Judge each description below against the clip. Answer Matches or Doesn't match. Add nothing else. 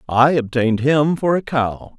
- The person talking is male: Matches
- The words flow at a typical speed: Matches